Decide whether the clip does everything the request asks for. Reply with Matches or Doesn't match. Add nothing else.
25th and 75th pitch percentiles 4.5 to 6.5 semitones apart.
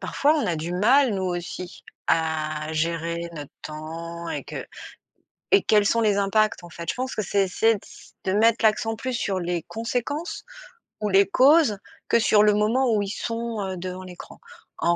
Matches